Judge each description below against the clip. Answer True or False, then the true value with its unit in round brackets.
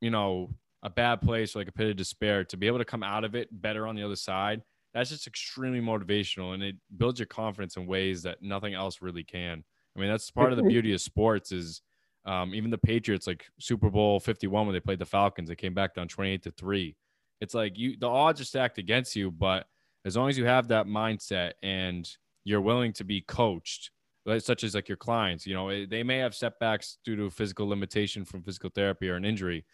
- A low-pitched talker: True (105 Hz)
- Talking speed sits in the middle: False (235 wpm)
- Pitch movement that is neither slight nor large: True (3.0 semitones)